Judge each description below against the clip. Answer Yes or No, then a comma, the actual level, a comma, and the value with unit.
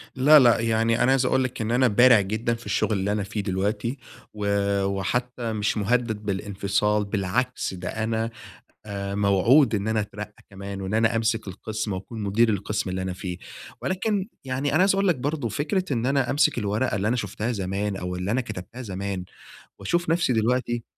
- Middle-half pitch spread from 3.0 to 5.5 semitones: Yes, average, 3.8 semitones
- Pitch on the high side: No, low, 110 Hz